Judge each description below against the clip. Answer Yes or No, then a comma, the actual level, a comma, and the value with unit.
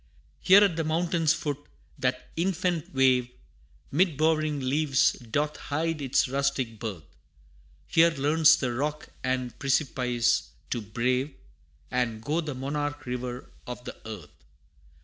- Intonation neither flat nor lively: Yes, average, 3.8 semitones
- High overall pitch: No, medium, 140 Hz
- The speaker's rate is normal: No, slow, 130 wpm